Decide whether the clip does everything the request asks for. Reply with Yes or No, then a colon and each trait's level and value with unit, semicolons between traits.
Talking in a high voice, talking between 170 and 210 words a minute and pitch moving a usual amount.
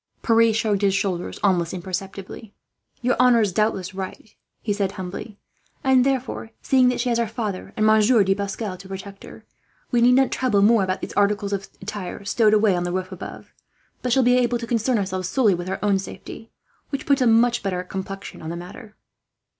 Yes: high, 205 Hz; average, 200 wpm; average, 3.5 semitones